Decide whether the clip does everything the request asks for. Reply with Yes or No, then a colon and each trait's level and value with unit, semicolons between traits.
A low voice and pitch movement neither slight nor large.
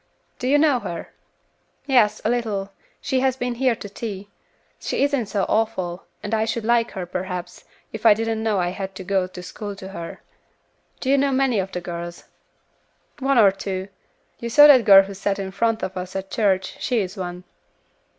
No: high, 205 Hz; average, 3.8 semitones